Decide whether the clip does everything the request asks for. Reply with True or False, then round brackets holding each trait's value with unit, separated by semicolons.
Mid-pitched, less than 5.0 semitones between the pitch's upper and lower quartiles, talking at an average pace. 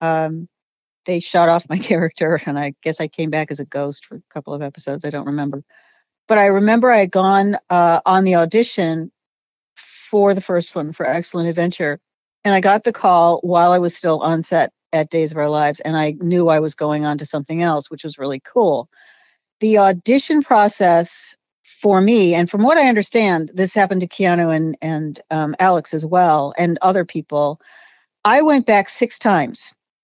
True (170 Hz; 3.6 semitones; 195 wpm)